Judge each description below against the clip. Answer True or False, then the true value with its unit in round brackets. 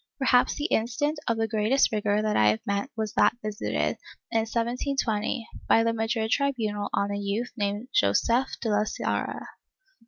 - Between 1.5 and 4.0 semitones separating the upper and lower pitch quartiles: True (2.8 semitones)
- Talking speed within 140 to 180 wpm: True (165 wpm)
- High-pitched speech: True (220 Hz)